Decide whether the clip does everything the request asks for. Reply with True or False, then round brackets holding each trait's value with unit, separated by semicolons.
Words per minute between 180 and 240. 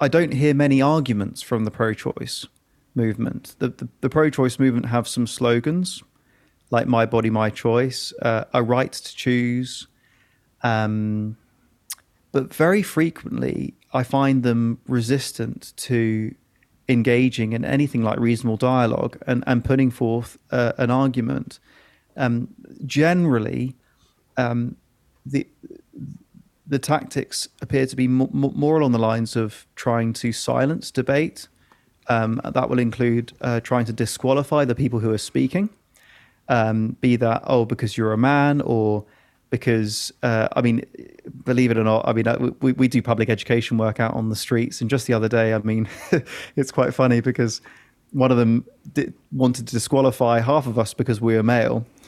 False (155 wpm)